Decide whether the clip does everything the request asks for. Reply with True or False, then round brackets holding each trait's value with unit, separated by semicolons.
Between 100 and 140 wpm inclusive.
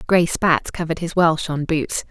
False (200 wpm)